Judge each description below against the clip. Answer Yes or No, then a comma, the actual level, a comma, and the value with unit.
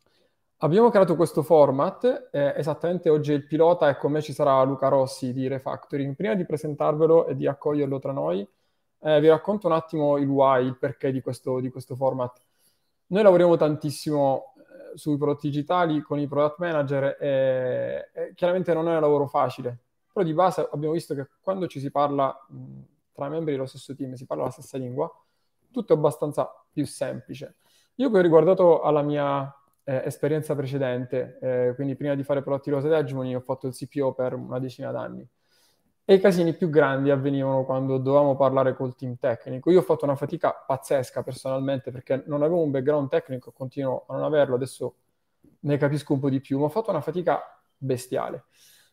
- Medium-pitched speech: Yes, medium, 145 Hz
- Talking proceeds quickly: Yes, fast, 190 wpm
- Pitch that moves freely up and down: No, average, 3.1 semitones